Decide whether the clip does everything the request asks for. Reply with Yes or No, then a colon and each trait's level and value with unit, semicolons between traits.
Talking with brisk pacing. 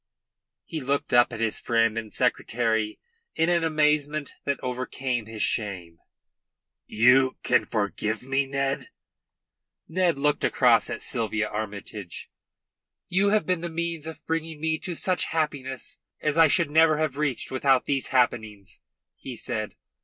No: average, 145 wpm